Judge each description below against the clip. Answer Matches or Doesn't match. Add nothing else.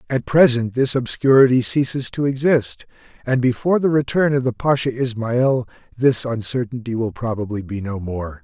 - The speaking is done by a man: Matches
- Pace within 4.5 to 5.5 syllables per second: Matches